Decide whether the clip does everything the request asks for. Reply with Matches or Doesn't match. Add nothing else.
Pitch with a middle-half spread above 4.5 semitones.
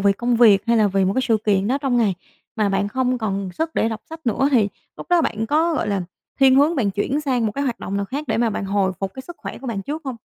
Matches